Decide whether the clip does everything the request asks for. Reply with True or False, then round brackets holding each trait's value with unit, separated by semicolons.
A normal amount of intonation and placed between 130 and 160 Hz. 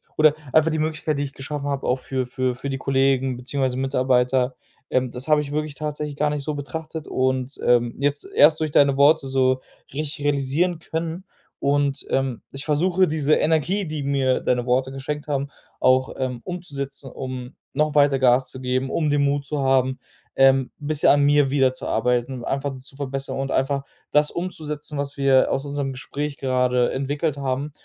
False (2.2 semitones; 140 Hz)